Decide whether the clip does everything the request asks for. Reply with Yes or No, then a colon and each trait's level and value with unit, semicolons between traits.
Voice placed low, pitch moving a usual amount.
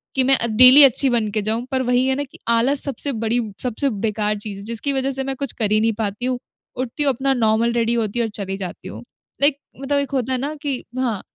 No: high, 245 Hz; average, 3.5 semitones